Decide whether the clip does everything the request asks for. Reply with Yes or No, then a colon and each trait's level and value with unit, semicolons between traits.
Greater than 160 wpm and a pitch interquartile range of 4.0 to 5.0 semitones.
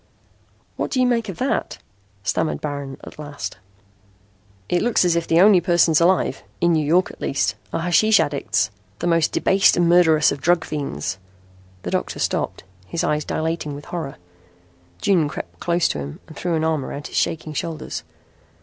No: average, 175 wpm; average, 3.3 semitones